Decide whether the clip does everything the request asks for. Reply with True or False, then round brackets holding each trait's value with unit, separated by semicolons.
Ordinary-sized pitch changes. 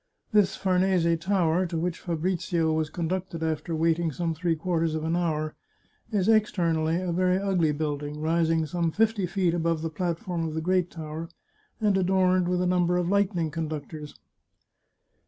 False (2.3 semitones)